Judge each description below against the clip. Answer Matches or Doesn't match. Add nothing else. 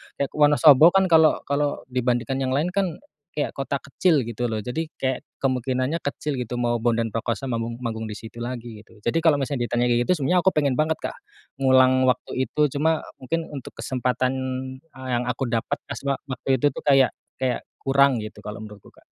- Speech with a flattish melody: Doesn't match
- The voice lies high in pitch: Doesn't match